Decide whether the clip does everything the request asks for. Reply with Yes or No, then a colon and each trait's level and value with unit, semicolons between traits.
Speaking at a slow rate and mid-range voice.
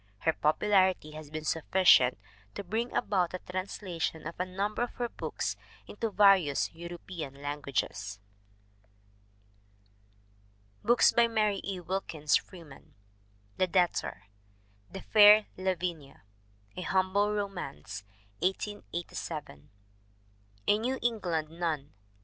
Yes: slow, 110 wpm; medium, 180 Hz